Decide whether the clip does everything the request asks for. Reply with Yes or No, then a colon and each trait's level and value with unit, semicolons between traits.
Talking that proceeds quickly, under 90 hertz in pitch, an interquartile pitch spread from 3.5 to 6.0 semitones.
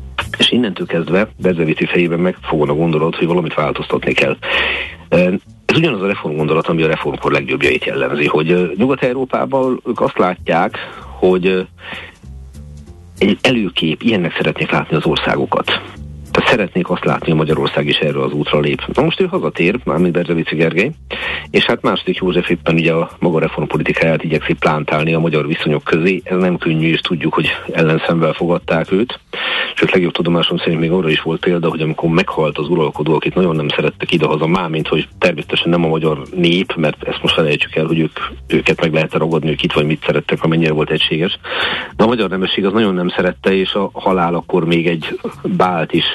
No: fast, 180 wpm; very low, 80 Hz; narrow, 2.4 semitones